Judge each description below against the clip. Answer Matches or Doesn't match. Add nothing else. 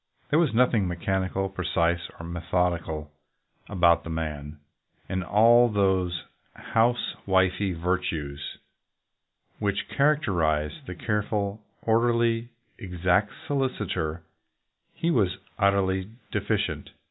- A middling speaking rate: Doesn't match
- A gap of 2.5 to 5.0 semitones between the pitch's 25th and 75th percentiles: Matches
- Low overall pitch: Matches